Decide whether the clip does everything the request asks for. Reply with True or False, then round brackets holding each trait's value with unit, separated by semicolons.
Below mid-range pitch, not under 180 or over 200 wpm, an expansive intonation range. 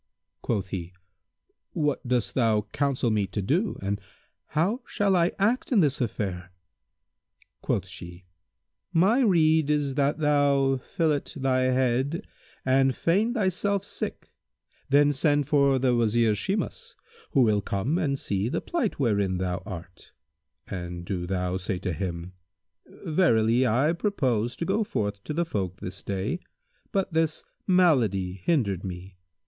False (130 Hz; 140 wpm; 8.5 semitones)